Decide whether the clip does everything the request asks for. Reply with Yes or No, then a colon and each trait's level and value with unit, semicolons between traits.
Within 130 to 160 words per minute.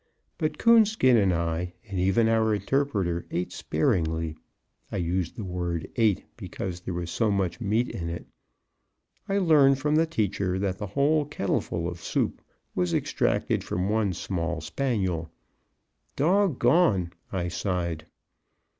Yes: average, 140 wpm